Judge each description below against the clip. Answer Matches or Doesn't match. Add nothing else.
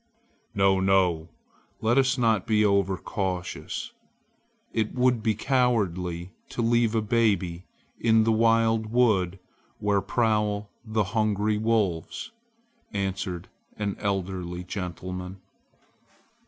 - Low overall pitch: Matches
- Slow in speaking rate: Matches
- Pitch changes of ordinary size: Matches